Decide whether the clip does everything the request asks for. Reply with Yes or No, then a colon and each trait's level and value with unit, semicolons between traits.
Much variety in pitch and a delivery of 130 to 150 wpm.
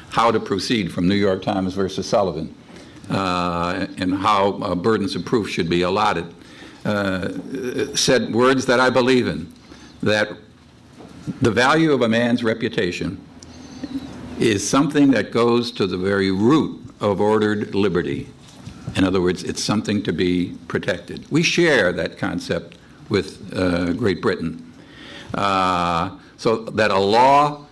Yes: wide, 5.7 semitones; average, 140 wpm